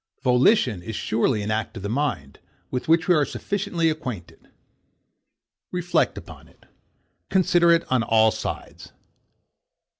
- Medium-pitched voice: No, low, 130 Hz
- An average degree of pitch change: No, wide, 7.6 semitones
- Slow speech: Yes, slow, 130 wpm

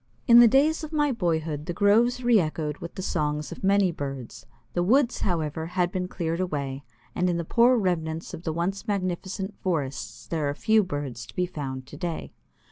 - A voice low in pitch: No, medium, 175 Hz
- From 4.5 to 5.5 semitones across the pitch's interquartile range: Yes, average, 4.8 semitones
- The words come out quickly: No, average, 195 wpm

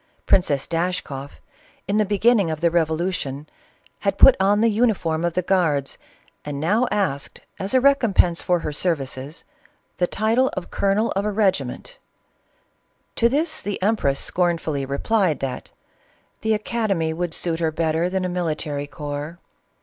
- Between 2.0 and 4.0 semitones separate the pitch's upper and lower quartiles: No, average, 4.9 semitones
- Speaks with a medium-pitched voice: Yes, medium, 175 Hz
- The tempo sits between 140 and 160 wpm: Yes, average, 155 wpm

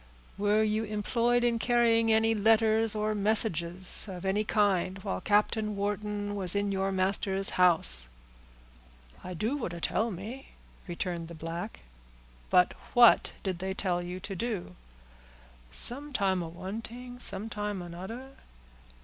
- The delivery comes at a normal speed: No, slow, 130 wpm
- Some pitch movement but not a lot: Yes, average, 3.4 semitones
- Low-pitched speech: No, high, 205 Hz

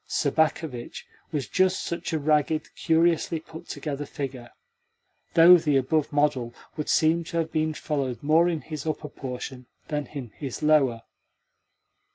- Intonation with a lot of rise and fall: No, average, 2.8 semitones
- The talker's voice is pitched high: No, medium, 150 Hz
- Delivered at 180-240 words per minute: No, average, 145 wpm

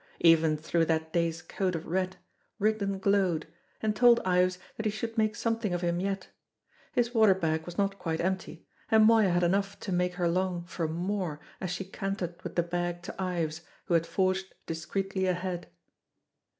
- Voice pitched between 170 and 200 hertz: Yes, medium, 185 Hz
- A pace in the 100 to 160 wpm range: No, average, 180 wpm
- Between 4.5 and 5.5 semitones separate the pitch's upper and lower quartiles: No, narrow, 2.5 semitones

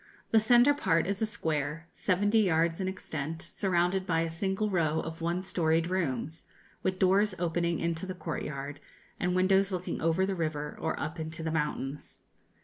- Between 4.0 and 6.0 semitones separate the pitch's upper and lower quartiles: No, average, 2.9 semitones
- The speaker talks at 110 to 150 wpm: No, average, 170 wpm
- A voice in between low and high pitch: Yes, medium, 170 Hz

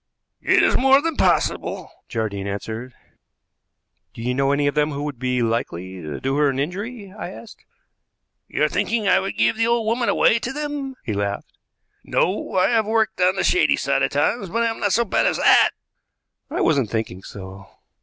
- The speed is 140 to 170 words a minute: No, average, 195 wpm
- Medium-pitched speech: Yes, medium, 170 Hz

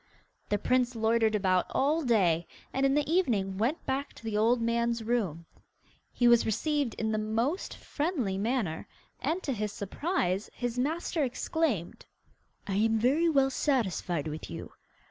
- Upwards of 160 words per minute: No, average, 155 wpm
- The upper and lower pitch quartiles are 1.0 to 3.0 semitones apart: No, average, 4.7 semitones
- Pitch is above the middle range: Yes, high, 235 Hz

